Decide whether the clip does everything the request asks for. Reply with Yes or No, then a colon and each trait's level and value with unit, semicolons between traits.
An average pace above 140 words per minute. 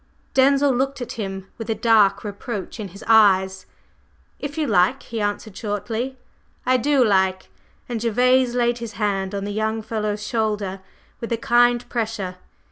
Yes: average, 160 wpm